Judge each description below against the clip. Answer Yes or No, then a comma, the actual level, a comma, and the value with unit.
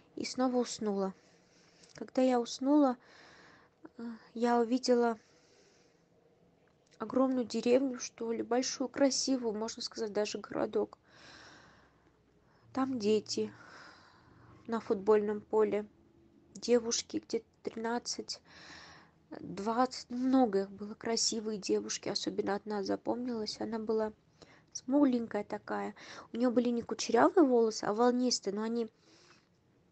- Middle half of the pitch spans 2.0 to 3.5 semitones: Yes, average, 3.0 semitones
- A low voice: No, high, 230 Hz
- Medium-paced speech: No, slow, 95 wpm